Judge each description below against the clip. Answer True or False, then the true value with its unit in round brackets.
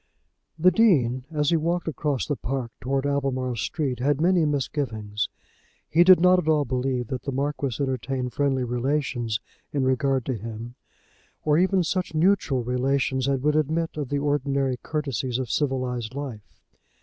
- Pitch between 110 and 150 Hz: True (135 Hz)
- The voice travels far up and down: False (3.1 semitones)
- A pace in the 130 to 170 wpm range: True (160 wpm)